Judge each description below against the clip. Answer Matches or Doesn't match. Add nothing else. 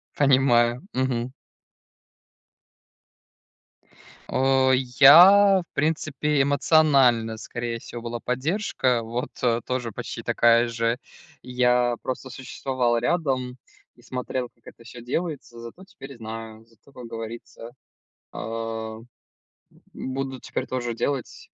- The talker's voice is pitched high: Doesn't match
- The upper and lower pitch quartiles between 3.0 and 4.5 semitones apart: Doesn't match